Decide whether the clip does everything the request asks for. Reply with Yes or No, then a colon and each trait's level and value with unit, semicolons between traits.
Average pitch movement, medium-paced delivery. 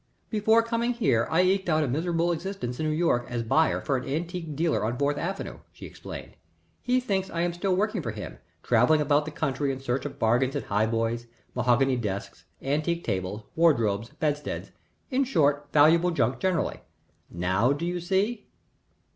No: wide, 6.3 semitones; average, 180 wpm